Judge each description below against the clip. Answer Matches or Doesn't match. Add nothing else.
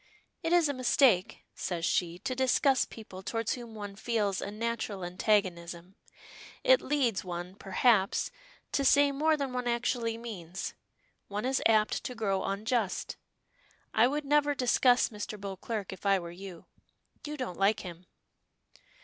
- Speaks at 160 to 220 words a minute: Doesn't match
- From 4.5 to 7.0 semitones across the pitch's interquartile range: Matches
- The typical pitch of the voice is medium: Doesn't match